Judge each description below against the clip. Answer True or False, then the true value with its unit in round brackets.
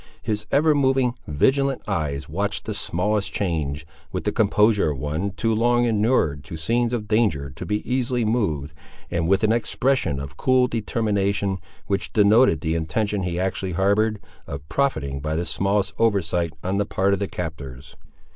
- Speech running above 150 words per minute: True (165 wpm)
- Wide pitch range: True (5.9 semitones)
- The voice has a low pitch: True (100 Hz)